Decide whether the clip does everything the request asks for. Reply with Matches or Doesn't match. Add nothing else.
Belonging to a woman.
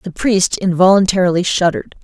Matches